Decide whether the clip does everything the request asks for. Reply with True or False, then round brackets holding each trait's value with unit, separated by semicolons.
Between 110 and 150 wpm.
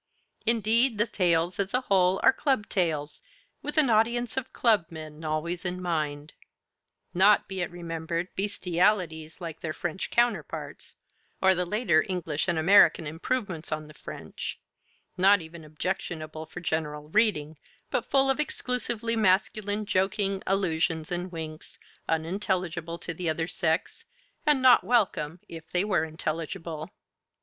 True (140 wpm)